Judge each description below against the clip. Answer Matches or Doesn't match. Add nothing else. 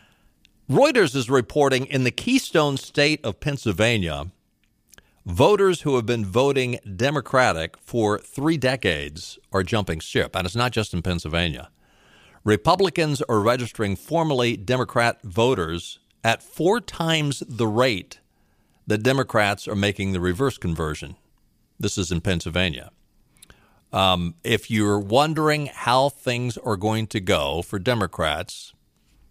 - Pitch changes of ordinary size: Doesn't match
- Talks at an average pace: Doesn't match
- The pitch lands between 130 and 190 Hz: Doesn't match